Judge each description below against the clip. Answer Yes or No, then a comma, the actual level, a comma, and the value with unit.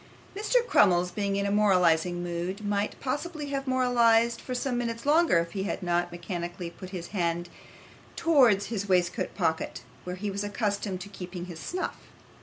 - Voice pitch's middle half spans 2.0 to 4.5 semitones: No, average, 5.1 semitones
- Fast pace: No, average, 170 wpm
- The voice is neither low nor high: No, high, 200 Hz